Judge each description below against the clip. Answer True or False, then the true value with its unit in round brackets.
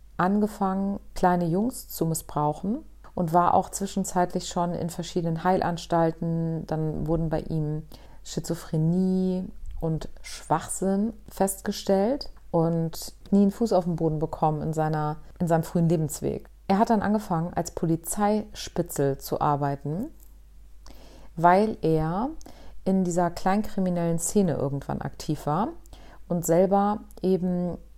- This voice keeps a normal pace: False (120 wpm)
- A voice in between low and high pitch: True (175 Hz)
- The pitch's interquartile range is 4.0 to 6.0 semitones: False (3.4 semitones)